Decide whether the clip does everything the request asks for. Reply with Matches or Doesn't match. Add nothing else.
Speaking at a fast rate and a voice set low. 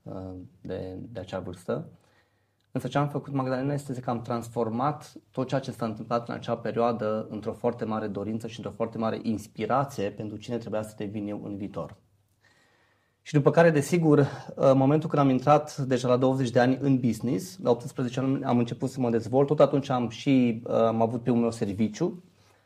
Matches